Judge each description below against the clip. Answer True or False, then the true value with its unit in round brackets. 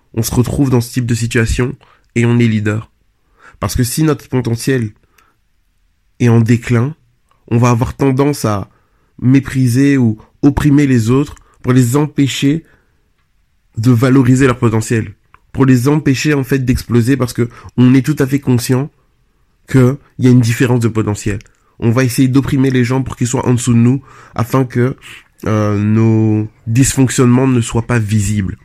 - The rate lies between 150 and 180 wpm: True (170 wpm)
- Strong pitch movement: False (3.1 semitones)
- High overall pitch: False (125 Hz)